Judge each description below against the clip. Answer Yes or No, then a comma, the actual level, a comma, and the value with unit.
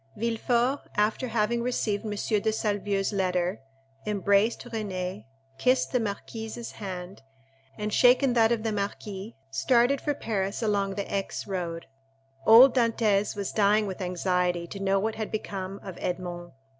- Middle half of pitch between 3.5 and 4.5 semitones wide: No, average, 2.8 semitones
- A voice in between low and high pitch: No, high, 205 Hz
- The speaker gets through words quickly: No, average, 145 wpm